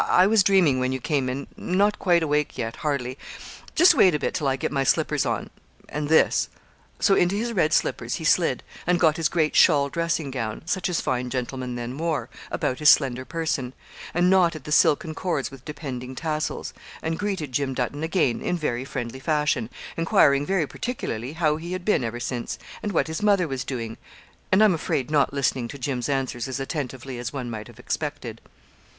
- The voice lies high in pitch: No, medium, 145 Hz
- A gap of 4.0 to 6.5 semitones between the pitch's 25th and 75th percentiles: Yes, average, 4.6 semitones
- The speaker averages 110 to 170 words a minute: No, average, 200 wpm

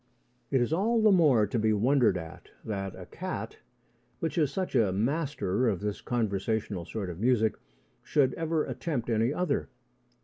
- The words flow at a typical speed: Yes, average, 165 wpm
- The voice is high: No, low, 120 Hz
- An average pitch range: No, wide, 6.2 semitones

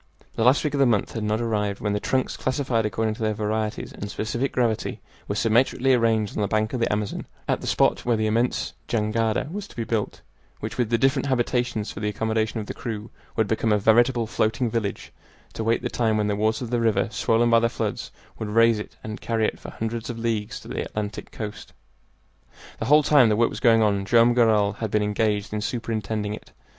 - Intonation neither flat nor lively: No, narrow, 1.8 semitones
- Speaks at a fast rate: Yes, fast, 225 wpm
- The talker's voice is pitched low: Yes, low, 110 Hz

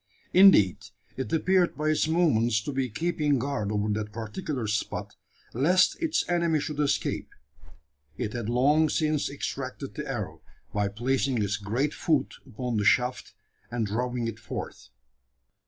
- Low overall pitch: Yes, low, 130 Hz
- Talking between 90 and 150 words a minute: Yes, average, 145 wpm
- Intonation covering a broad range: Yes, wide, 5.9 semitones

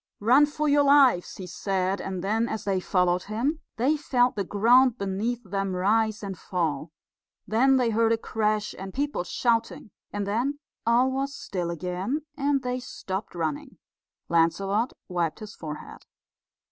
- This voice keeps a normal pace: Yes, average, 155 wpm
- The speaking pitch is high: Yes, high, 215 Hz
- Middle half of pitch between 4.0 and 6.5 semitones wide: Yes, average, 5.1 semitones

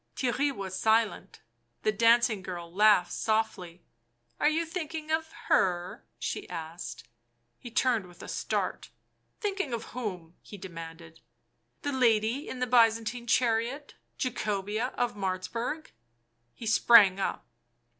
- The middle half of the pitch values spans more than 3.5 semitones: Yes, wide, 5.4 semitones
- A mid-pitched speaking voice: No, high, 220 Hz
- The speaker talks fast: No, average, 145 wpm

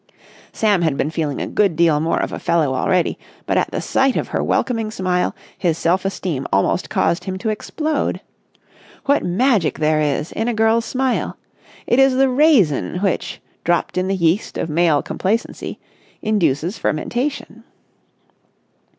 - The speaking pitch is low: No, medium, 185 Hz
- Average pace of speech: Yes, average, 155 wpm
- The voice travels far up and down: Yes, wide, 5.9 semitones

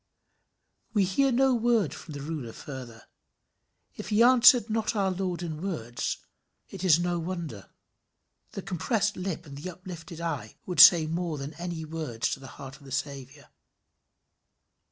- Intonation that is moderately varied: Yes, average, 5.0 semitones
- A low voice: No, medium, 170 Hz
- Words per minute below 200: Yes, average, 160 wpm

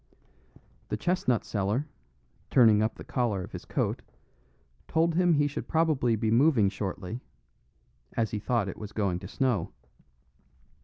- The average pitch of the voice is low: Yes, low, 115 Hz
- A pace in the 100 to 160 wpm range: Yes, average, 145 wpm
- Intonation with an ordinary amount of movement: No, wide, 5.7 semitones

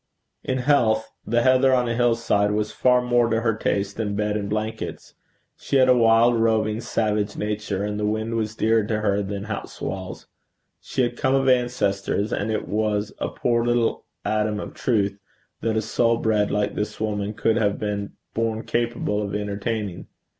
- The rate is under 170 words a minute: No, average, 185 wpm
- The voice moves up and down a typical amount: No, narrow, 2.1 semitones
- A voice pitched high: No, low, 110 Hz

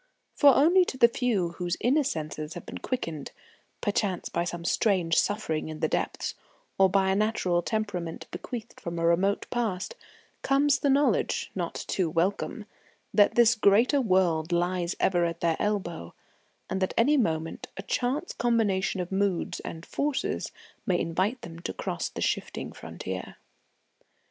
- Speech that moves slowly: No, average, 155 wpm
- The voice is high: Yes, high, 195 Hz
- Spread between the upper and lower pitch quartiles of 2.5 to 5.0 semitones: No, wide, 5.5 semitones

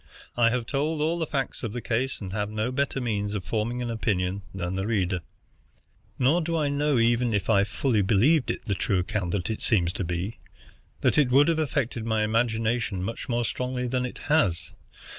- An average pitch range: Yes, average, 4.4 semitones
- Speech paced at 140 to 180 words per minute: No, average, 200 wpm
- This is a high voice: No, low, 115 Hz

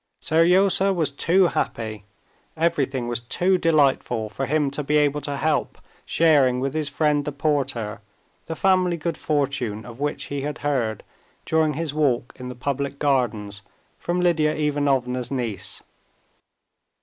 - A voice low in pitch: No, medium, 145 Hz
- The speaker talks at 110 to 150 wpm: Yes, average, 145 wpm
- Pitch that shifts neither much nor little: Yes, average, 3.8 semitones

